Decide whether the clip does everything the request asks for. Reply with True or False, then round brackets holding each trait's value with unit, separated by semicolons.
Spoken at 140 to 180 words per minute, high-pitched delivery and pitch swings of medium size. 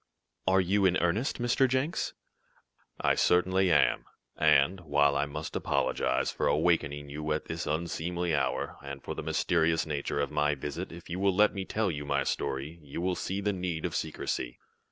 False (175 wpm; 85 Hz; 4.3 semitones)